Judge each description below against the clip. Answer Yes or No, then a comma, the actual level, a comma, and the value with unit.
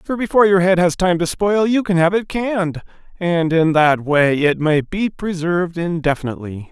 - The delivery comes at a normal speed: Yes, average, 195 wpm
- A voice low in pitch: No, medium, 175 Hz